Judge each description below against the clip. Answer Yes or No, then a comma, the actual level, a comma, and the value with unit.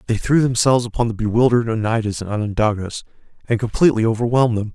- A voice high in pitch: No, low, 115 Hz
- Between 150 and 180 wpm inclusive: Yes, average, 165 wpm